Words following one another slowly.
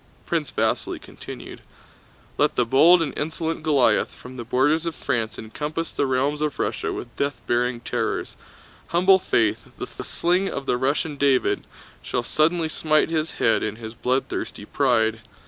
No: average, 155 wpm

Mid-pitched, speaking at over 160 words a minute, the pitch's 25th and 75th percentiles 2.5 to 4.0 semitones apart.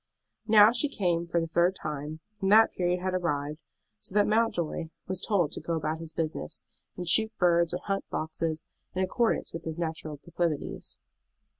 Yes: medium, 170 Hz; average, 175 wpm; average, 2.9 semitones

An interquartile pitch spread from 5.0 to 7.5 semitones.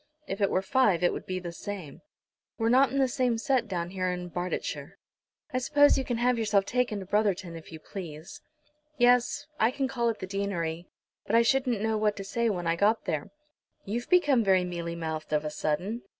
Yes: wide, 5.4 semitones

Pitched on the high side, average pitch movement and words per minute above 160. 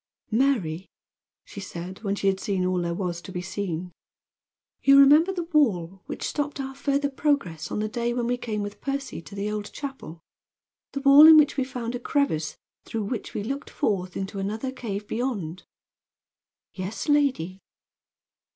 No: high, 215 Hz; wide, 6.7 semitones; average, 170 wpm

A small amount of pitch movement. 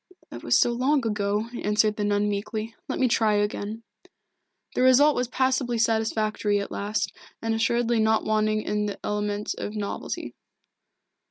Yes: narrow, 2.0 semitones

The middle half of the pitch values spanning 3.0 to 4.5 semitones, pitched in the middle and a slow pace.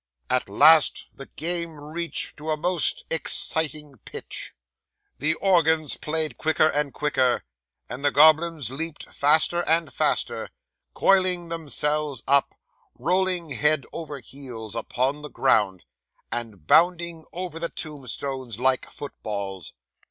Yes: average, 3.7 semitones; medium, 150 Hz; slow, 120 wpm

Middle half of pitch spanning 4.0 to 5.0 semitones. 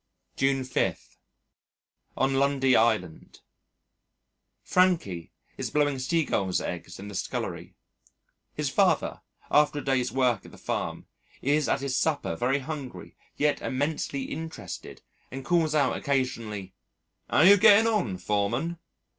Yes: average, 4.6 semitones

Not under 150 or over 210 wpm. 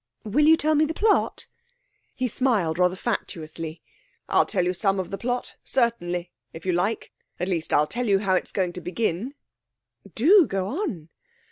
Yes: average, 175 wpm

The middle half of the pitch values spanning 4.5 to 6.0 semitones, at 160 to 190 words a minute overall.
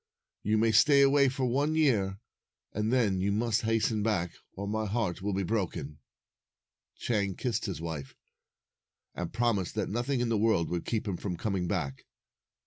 No: average, 3.8 semitones; average, 175 wpm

